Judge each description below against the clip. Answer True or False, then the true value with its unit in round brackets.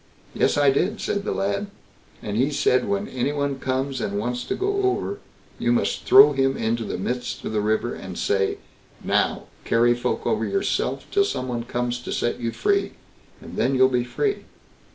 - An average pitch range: False (8.9 semitones)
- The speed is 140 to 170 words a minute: False (195 wpm)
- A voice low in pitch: True (130 Hz)